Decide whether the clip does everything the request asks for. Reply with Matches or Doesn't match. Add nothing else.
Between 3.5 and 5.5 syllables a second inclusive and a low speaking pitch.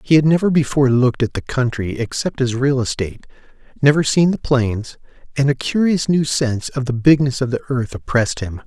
Doesn't match